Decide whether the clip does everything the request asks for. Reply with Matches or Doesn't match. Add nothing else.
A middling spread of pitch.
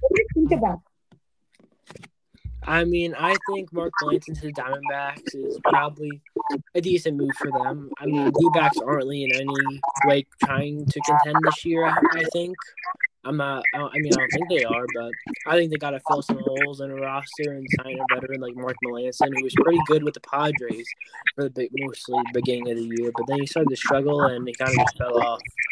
Matches